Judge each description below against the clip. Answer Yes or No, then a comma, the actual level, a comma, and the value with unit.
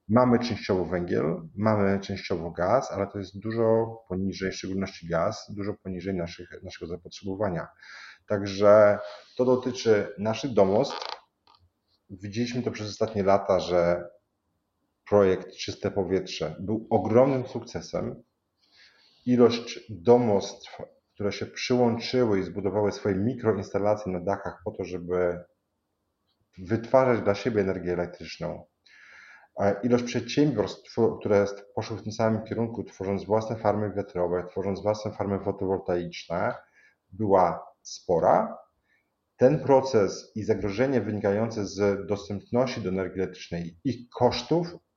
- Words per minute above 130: No, average, 115 wpm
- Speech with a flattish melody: No, average, 3.0 semitones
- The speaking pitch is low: Yes, low, 105 Hz